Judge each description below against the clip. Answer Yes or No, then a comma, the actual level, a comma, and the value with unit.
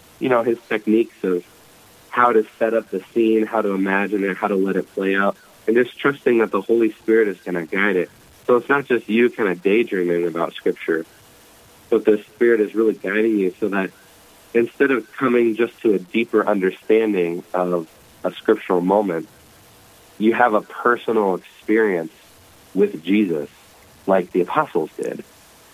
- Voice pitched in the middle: No, low, 105 Hz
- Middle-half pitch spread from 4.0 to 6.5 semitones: No, average, 2.9 semitones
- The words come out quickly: No, average, 175 wpm